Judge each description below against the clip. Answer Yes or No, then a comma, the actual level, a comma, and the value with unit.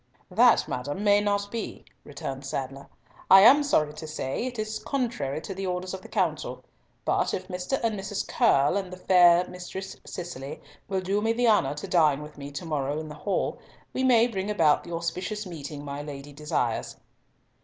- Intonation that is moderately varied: No, wide, 5.7 semitones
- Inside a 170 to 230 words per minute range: Yes, average, 190 wpm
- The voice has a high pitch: No, medium, 180 Hz